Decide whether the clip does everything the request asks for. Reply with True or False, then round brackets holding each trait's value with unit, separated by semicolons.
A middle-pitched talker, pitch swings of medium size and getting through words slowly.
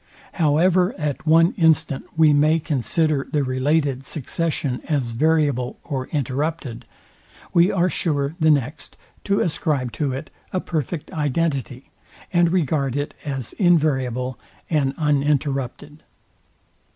True (150 Hz; 3.2 semitones; 115 wpm)